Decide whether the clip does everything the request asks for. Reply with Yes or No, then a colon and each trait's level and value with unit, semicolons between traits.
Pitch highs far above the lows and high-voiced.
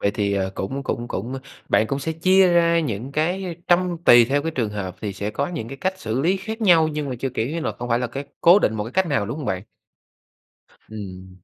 No: wide, 7.7 semitones; low, 135 Hz